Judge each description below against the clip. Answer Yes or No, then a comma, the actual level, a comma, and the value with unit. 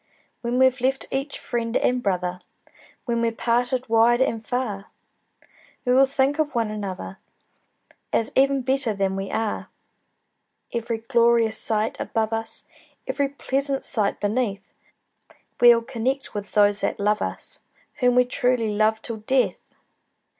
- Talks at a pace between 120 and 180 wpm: Yes, average, 140 wpm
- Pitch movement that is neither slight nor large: Yes, average, 3.1 semitones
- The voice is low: No, high, 235 Hz